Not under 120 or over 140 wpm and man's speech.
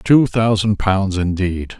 Yes: slow, 135 wpm; male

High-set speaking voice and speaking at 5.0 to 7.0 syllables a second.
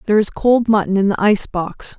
Yes: high, 205 Hz; 6.1 syllables/s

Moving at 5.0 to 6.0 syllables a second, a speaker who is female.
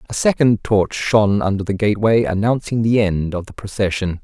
No: 5.5 syllables/s; male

